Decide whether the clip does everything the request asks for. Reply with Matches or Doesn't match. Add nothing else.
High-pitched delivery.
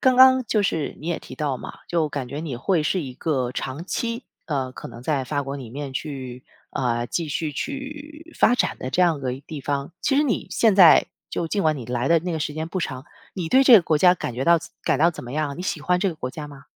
Doesn't match